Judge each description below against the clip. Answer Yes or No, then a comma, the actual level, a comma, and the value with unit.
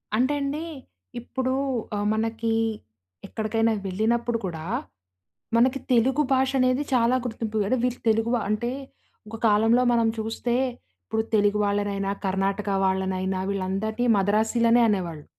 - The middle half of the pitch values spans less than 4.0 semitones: Yes, average, 3.0 semitones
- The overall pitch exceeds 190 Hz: Yes, high, 220 Hz